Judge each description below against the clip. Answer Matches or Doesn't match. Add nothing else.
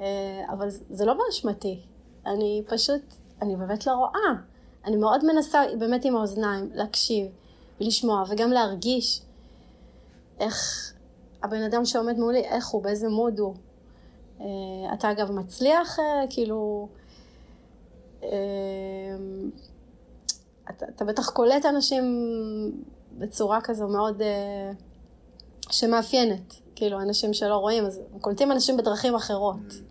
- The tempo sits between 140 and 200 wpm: Doesn't match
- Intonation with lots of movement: Doesn't match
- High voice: Matches